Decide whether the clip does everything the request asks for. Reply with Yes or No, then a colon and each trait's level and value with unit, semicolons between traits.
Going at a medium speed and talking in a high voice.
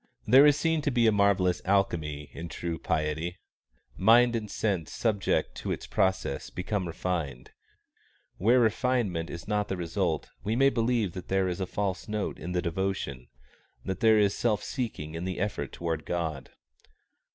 No: average, 165 wpm; very low, 95 Hz